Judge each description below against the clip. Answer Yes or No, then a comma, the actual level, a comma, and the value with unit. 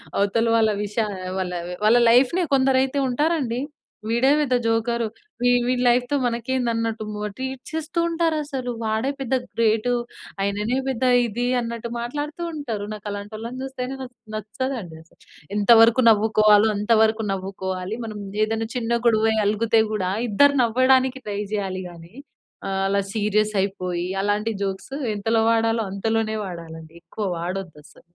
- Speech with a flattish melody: No, average, 3.4 semitones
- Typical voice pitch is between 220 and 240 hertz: Yes, high, 225 Hz